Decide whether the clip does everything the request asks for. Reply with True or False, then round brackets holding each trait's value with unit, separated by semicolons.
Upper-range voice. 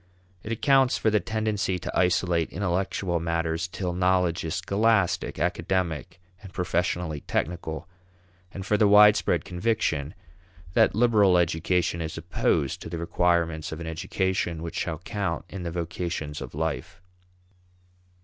False (90 Hz)